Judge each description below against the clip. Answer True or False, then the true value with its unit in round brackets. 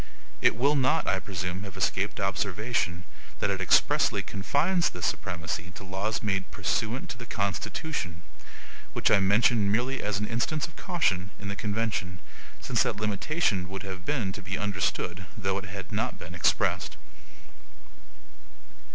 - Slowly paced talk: False (150 wpm)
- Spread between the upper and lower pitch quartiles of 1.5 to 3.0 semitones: False (3.7 semitones)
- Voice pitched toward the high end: False (100 Hz)